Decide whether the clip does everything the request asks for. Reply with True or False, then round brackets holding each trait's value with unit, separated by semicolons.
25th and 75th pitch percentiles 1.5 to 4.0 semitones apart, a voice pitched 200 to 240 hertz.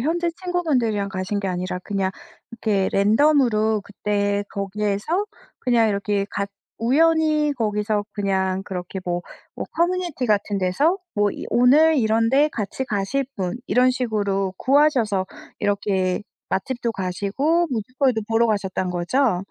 False (5.1 semitones; 215 Hz)